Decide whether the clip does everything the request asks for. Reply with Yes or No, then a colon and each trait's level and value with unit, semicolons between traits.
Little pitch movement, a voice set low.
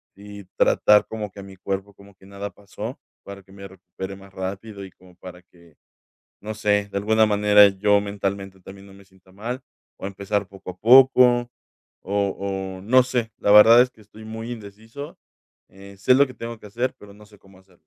Yes: narrow, 2.1 semitones; low, 100 Hz